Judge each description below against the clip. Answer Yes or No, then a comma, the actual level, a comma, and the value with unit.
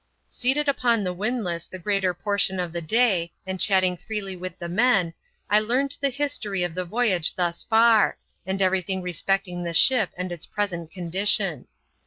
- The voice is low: No, high, 190 Hz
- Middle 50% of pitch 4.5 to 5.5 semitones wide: No, average, 3.7 semitones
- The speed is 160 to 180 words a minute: Yes, average, 175 wpm